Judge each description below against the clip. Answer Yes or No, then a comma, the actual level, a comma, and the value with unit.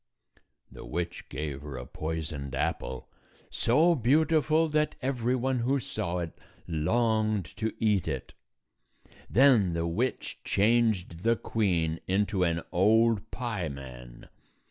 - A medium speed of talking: No, slow, 120 wpm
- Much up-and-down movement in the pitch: Yes, wide, 6.5 semitones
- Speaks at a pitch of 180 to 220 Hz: No, low, 105 Hz